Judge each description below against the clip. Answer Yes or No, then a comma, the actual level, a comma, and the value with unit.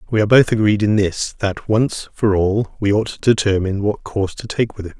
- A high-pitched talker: No, low, 105 Hz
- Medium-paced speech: No, fast, 240 wpm